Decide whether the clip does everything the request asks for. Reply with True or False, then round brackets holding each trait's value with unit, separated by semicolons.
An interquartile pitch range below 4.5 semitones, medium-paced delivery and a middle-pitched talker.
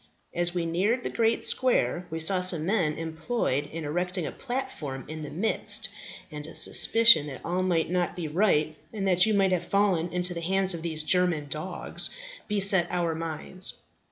True (3.2 semitones; 185 wpm; 175 Hz)